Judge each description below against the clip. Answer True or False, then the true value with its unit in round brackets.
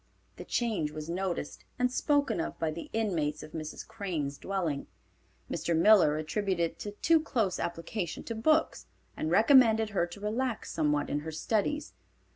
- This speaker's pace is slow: False (165 wpm)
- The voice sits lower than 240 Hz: True (190 Hz)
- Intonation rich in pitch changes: True (6.0 semitones)